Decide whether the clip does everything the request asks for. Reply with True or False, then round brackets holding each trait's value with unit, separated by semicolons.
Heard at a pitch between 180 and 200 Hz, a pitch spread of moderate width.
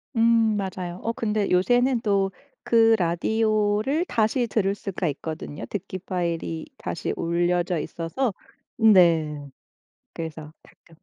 True (190 Hz; 4.5 semitones)